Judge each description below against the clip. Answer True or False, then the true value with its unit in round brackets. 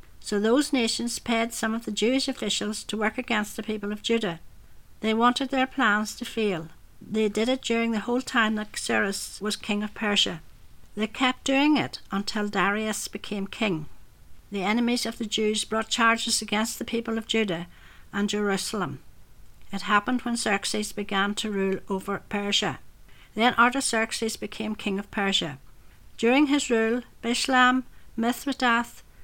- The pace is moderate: True (160 wpm)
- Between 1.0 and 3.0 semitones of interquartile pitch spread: True (2.5 semitones)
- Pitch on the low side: False (215 Hz)